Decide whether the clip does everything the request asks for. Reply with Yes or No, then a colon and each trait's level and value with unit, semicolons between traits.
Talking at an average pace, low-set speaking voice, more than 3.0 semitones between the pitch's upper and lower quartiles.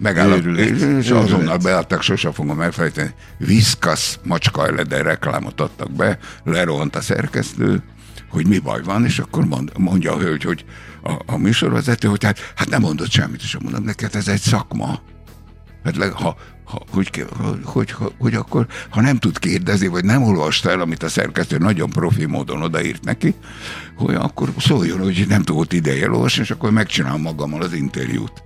No: fast, 170 wpm; low, 100 Hz; average, 4.4 semitones